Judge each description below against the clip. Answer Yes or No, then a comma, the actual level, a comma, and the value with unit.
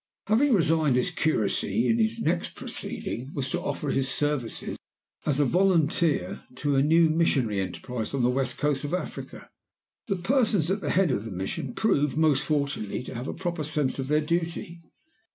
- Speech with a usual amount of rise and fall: Yes, average, 4.7 semitones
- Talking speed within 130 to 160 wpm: No, average, 170 wpm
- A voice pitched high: No, medium, 150 Hz